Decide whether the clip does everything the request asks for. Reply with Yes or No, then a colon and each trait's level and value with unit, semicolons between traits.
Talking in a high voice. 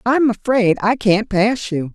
Yes: high, 220 Hz